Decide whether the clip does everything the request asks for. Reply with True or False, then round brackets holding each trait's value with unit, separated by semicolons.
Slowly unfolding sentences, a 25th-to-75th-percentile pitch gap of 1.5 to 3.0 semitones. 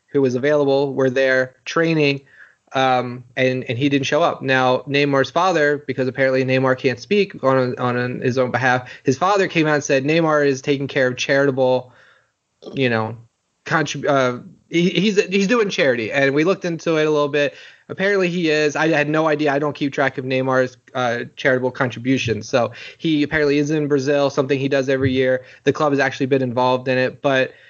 False (200 wpm; 2.4 semitones)